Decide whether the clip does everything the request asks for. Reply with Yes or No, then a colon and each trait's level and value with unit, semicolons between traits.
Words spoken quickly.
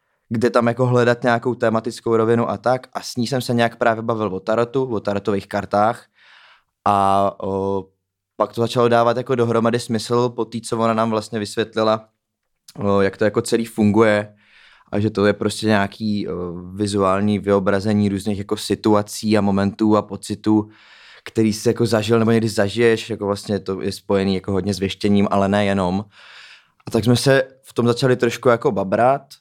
Yes: fast, 180 wpm